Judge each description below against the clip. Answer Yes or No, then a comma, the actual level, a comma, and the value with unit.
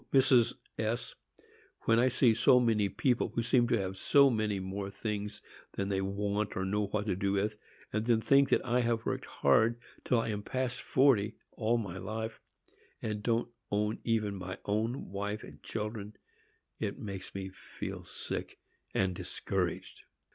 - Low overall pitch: Yes, low, 110 Hz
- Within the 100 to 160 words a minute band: No, average, 170 wpm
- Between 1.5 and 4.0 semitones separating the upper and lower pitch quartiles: Yes, average, 2.8 semitones